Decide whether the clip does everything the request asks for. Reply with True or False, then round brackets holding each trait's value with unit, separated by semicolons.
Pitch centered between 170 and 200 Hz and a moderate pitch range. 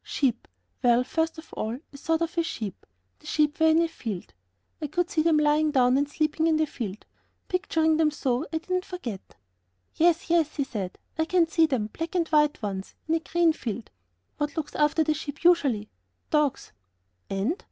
False (305 Hz; 4.4 semitones)